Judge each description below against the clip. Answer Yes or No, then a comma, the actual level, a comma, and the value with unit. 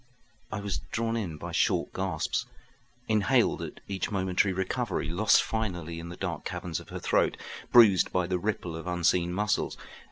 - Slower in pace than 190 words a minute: Yes, average, 165 wpm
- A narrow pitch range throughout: No, average, 3.1 semitones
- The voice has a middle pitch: No, very low, 95 Hz